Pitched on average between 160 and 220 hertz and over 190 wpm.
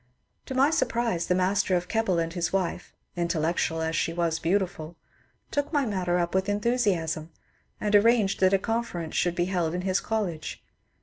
No: medium, 185 Hz; average, 175 wpm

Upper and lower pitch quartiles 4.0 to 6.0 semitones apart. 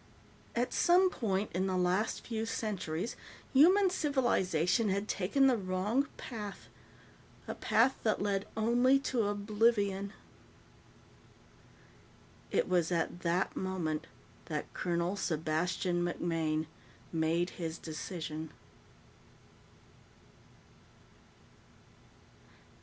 Yes: average, 4.8 semitones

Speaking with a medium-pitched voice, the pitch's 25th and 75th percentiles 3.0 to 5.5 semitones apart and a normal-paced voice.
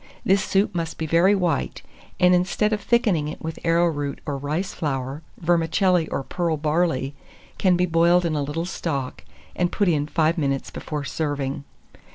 Yes: medium, 165 Hz; average, 3.4 semitones; average, 170 wpm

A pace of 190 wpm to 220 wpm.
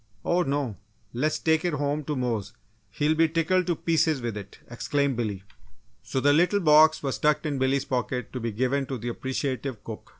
Yes: average, 200 wpm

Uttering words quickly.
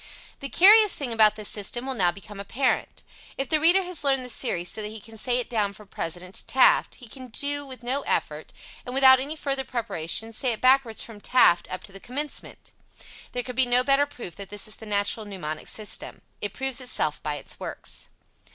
Yes: fast, 215 wpm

